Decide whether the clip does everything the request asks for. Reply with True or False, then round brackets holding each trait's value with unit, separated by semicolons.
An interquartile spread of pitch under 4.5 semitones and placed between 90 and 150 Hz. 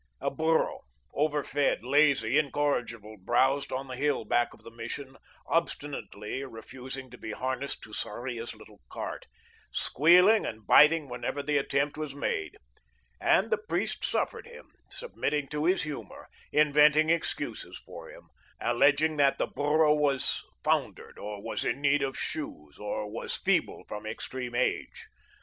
True (3.8 semitones; 140 Hz)